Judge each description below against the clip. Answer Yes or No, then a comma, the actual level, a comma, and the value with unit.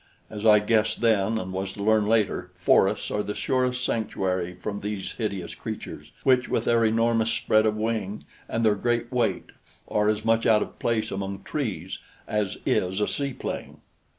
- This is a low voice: Yes, low, 110 Hz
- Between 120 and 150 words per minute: No, average, 175 wpm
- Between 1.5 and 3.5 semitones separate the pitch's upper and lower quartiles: Yes, narrow, 2.6 semitones